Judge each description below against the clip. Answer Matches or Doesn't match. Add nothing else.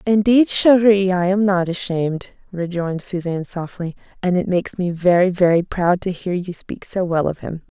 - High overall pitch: Doesn't match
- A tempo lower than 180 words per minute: Doesn't match